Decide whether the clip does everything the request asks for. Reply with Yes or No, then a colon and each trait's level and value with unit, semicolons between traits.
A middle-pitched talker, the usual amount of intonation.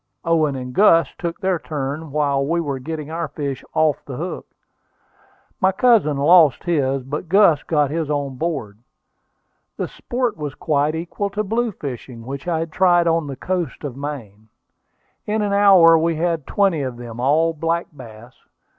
Yes: medium, 155 Hz; average, 3.8 semitones